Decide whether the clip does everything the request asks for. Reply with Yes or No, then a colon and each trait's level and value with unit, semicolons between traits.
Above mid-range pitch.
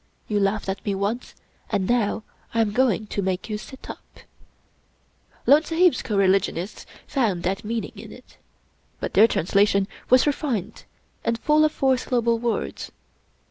Yes: high, 220 Hz